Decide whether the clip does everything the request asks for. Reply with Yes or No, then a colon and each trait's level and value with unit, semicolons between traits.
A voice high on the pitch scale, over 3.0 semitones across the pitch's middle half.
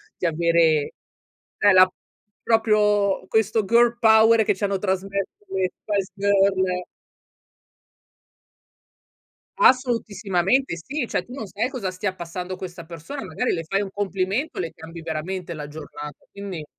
Yes: high, 195 Hz; average, 3.7 semitones